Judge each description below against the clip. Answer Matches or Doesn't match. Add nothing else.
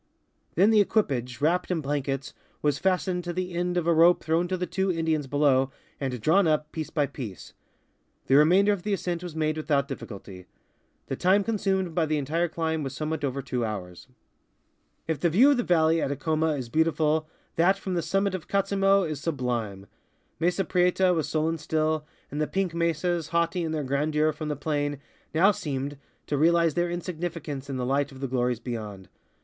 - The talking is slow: Doesn't match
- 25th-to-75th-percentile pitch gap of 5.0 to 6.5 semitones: Doesn't match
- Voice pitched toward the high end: Doesn't match